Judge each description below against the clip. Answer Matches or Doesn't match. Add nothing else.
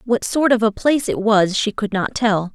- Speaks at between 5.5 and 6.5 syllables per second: Doesn't match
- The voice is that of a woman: Matches